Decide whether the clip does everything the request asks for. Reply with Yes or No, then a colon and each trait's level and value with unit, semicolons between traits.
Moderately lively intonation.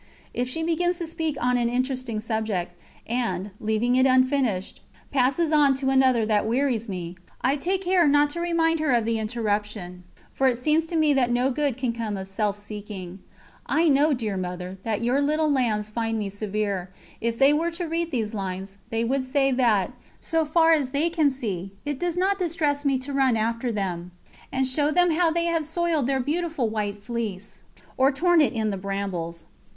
No: wide, 6.0 semitones